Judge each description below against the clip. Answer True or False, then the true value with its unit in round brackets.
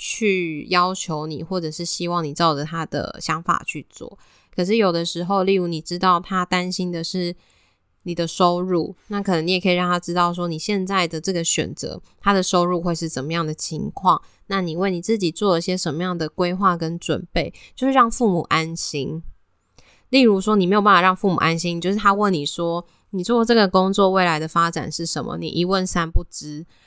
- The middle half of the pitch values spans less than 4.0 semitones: True (2.4 semitones)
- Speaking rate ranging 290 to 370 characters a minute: True (300 characters per minute)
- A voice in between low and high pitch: True (175 Hz)